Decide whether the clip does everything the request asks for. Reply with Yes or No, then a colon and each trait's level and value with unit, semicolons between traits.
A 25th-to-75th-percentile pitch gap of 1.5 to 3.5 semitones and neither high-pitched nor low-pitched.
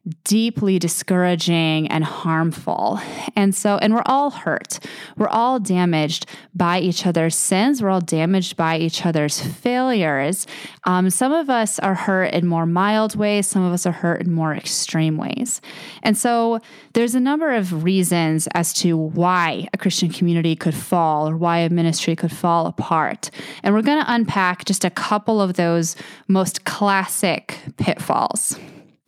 No: average, 4.1 semitones; medium, 180 Hz